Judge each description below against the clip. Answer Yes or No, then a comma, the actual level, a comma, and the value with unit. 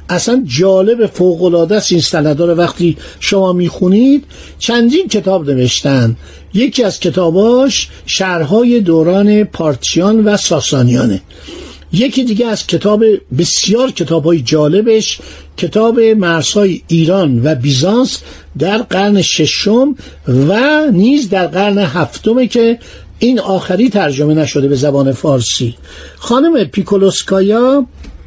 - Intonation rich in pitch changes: Yes, wide, 6.0 semitones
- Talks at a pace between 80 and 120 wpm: Yes, slow, 105 wpm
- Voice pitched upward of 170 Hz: Yes, high, 190 Hz